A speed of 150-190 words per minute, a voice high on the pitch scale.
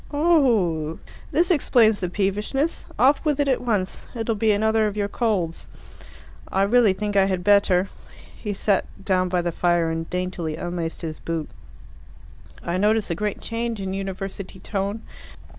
Yes: average, 160 wpm; high, 200 Hz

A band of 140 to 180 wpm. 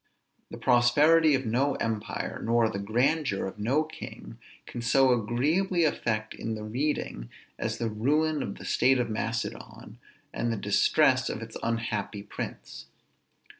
Yes: average, 145 wpm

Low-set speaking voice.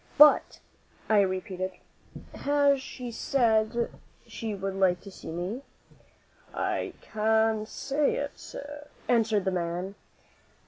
No: high, 220 Hz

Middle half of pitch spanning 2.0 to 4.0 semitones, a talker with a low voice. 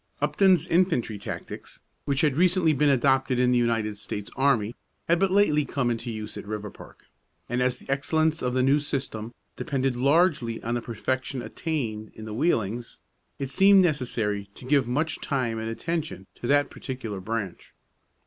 No: average, 4.7 semitones; low, 130 Hz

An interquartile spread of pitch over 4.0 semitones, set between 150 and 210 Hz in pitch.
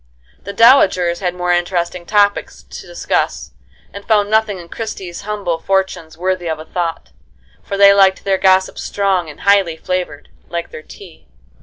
No: average, 2.7 semitones; medium, 185 Hz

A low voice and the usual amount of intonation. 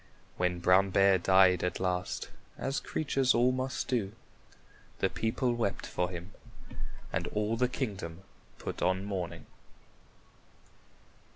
Yes: very low, 95 Hz; average, 4.6 semitones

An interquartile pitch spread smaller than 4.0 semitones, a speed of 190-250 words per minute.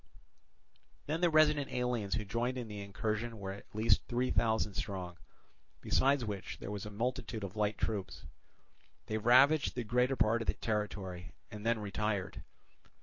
No: average, 3.3 semitones; average, 160 wpm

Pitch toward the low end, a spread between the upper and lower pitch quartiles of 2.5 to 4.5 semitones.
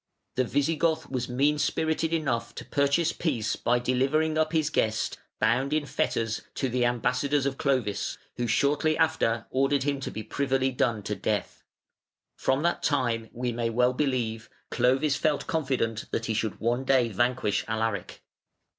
Yes: low, 130 Hz; average, 3.8 semitones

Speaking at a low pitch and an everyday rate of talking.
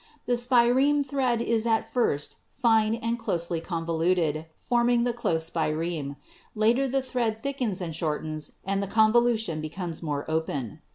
No: high, 215 Hz; average, 150 wpm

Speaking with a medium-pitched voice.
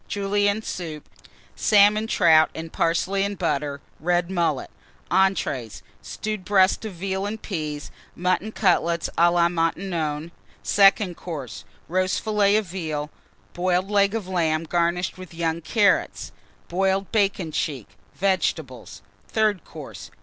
Yes: medium, 180 Hz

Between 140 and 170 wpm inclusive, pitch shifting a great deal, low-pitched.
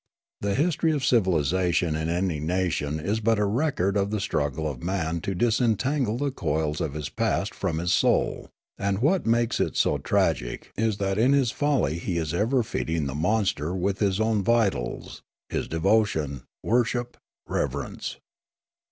Yes: average, 160 wpm; wide, 5.9 semitones; low, 100 Hz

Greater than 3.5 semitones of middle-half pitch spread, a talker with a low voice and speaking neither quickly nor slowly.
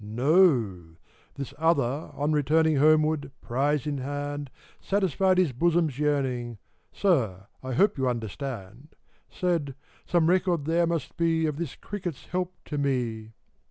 No: average, 4.5 semitones; medium, 145 Hz; average, 145 wpm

